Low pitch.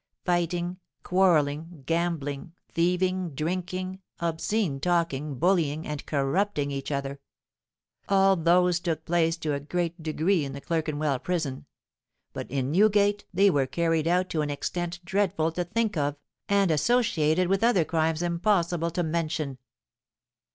No: medium, 170 Hz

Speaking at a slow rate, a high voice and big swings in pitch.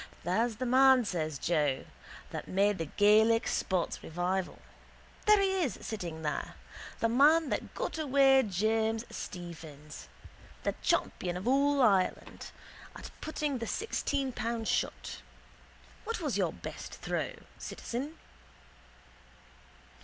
Yes: slow, 120 wpm; high, 225 Hz; wide, 7.0 semitones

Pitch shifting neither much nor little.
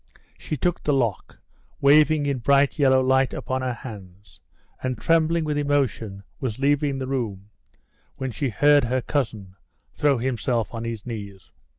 Yes: average, 4.1 semitones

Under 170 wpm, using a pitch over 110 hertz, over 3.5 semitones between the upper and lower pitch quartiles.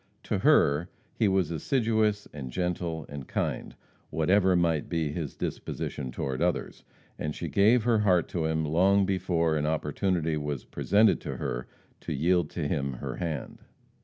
No: average, 160 wpm; very low, 85 Hz; average, 4.2 semitones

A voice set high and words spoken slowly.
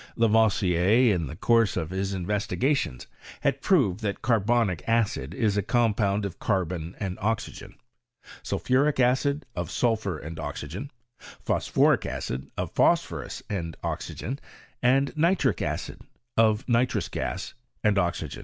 No: low, 105 Hz; slow, 125 wpm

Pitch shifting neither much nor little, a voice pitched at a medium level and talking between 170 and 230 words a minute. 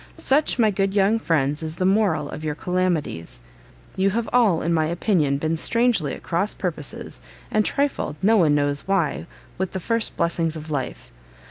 Yes: average, 5.0 semitones; medium, 175 Hz; average, 175 wpm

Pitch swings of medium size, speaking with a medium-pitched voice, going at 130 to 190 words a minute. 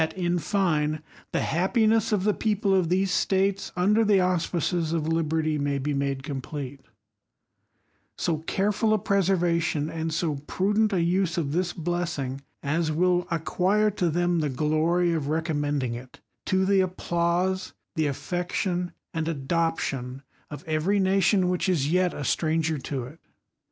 Yes: average, 3.5 semitones; medium, 170 Hz; average, 140 wpm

